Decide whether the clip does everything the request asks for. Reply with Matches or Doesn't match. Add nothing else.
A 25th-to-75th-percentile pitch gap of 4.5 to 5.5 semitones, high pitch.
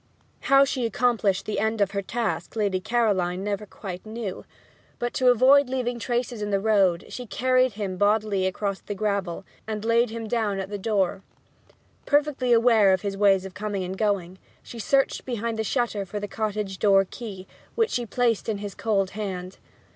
Doesn't match